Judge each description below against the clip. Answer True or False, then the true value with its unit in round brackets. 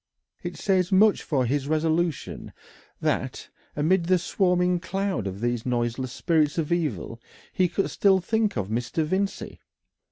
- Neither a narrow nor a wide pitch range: False (6.4 semitones)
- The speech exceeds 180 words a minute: False (140 wpm)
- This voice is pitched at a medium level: True (165 Hz)